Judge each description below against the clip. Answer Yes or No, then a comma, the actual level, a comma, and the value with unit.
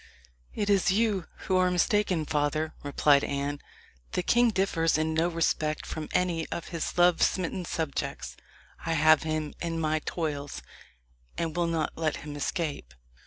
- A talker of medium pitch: Yes, medium, 165 Hz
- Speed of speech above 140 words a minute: Yes, average, 155 wpm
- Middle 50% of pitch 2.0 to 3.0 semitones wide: Yes, narrow, 2.6 semitones